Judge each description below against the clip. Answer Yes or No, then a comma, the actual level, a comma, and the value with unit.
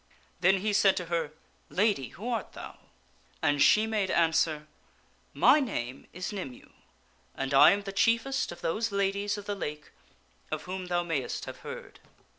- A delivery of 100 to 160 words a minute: No, average, 180 wpm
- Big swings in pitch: No, average, 4.2 semitones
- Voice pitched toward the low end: No, high, 190 Hz